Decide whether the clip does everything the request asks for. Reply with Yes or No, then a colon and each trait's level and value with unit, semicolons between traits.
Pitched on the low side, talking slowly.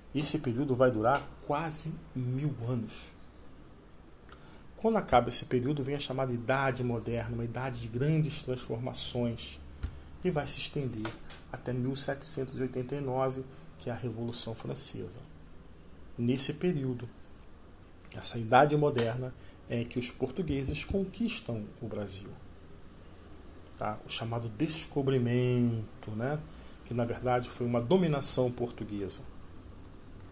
Yes: low, 125 Hz; slow, 110 wpm